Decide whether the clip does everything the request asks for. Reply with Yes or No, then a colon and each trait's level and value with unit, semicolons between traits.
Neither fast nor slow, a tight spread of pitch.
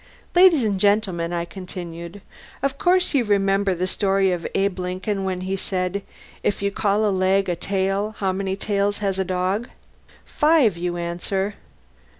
Yes: average, 160 wpm; narrow, 1.9 semitones